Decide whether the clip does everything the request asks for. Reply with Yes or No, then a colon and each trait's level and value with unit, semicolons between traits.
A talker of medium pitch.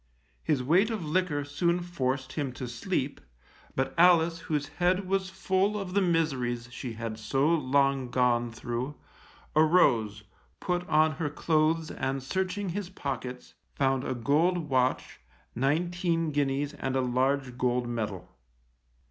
Yes: medium, 145 Hz